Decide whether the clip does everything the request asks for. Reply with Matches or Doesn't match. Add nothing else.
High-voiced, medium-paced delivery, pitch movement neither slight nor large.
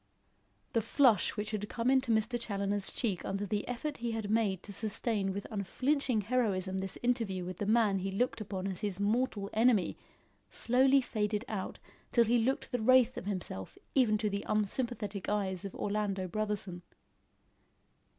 Matches